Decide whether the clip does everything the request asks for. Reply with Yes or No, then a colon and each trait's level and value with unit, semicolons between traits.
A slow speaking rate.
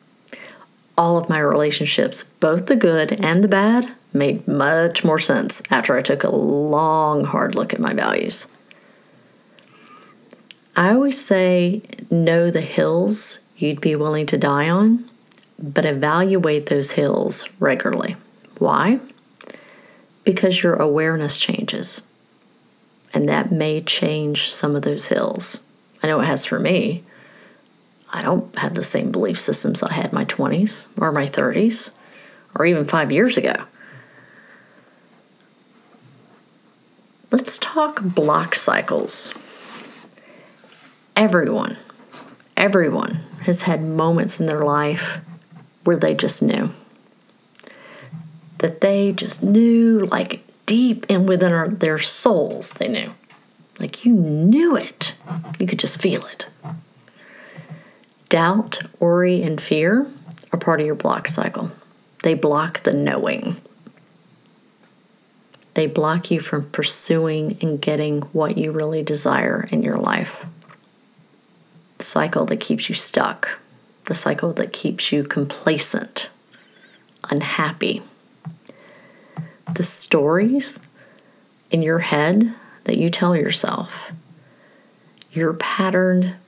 Yes: slow, 120 wpm